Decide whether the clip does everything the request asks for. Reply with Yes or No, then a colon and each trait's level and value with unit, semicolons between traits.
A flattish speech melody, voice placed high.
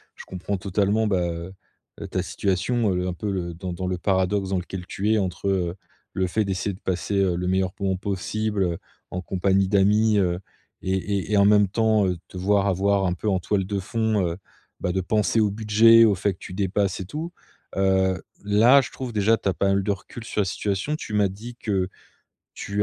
No: narrow, 2.1 semitones; low, 100 Hz